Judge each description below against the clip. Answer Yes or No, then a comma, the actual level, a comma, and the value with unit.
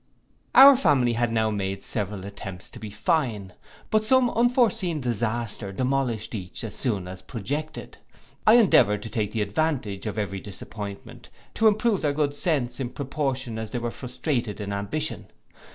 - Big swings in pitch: Yes, wide, 6.6 semitones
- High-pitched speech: No, low, 120 Hz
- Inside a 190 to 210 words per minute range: No, average, 160 wpm